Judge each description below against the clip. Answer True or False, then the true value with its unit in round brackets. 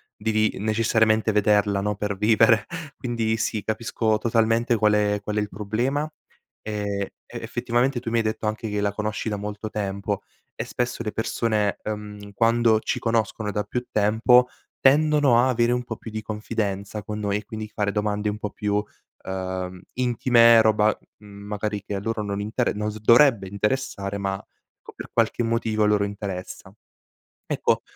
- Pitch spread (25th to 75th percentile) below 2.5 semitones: True (1.8 semitones)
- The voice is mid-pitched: False (110 Hz)